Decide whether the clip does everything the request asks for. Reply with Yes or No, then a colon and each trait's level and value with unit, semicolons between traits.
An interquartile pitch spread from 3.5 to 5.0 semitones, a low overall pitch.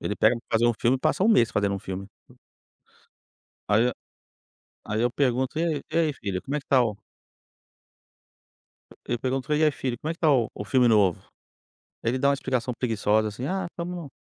Yes: average, 4.6 semitones; low, 125 Hz